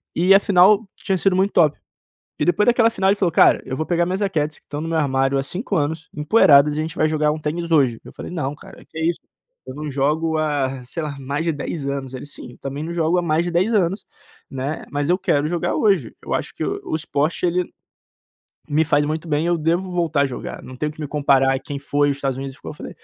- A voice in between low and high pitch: Yes, medium, 155 Hz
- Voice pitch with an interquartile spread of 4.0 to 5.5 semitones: No, average, 3.4 semitones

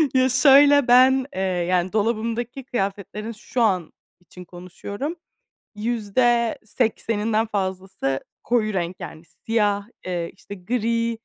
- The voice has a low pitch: No, high, 215 Hz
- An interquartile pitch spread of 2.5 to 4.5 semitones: Yes, average, 4.2 semitones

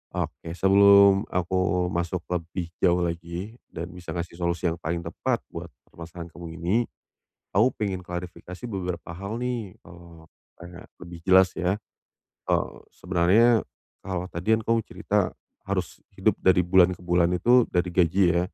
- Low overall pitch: Yes, very low, 90 Hz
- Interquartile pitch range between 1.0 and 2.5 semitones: Yes, narrow, 2.1 semitones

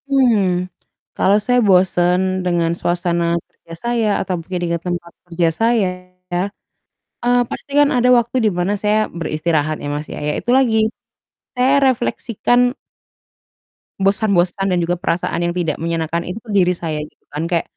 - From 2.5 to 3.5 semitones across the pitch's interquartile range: No, average, 5.0 semitones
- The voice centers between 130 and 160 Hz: No, medium, 180 Hz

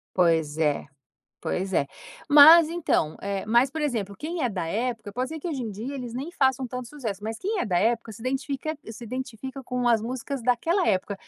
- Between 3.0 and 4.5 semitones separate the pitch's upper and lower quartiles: No, average, 5.1 semitones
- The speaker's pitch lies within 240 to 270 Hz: Yes, high, 245 Hz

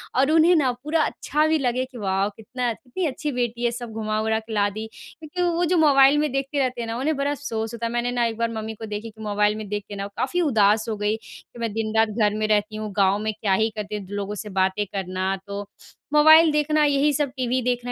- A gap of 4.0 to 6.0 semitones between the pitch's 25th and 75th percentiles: Yes, average, 4.5 semitones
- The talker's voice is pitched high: Yes, high, 230 Hz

